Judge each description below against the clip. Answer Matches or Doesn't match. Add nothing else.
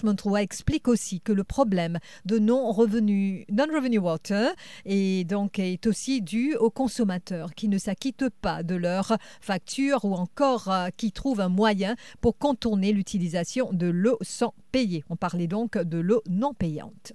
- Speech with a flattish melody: Doesn't match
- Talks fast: Doesn't match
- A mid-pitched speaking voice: Doesn't match